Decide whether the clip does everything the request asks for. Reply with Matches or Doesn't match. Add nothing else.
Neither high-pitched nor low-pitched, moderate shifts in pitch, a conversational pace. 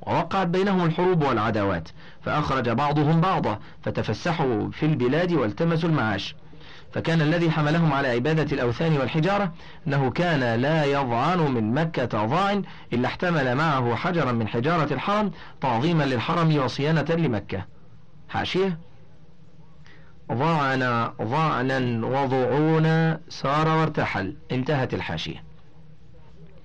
Matches